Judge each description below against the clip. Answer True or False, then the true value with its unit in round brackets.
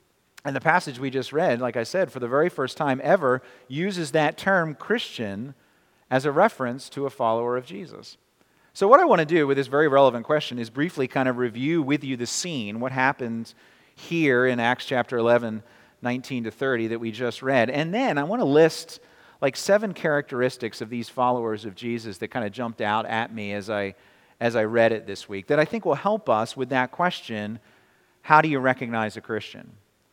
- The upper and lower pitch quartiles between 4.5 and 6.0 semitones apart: False (3.8 semitones)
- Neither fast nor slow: False (210 wpm)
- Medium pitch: False (125 Hz)